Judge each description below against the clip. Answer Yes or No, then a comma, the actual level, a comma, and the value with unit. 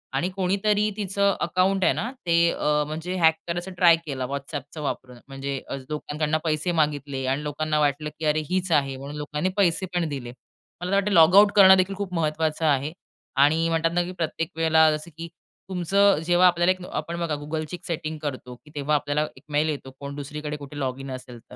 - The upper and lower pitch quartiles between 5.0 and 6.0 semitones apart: No, average, 3.4 semitones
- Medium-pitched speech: Yes, medium, 155 Hz